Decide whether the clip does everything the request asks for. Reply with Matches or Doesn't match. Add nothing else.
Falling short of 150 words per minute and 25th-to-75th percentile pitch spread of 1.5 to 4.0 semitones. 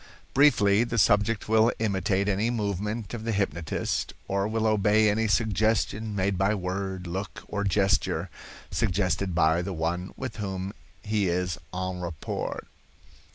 Matches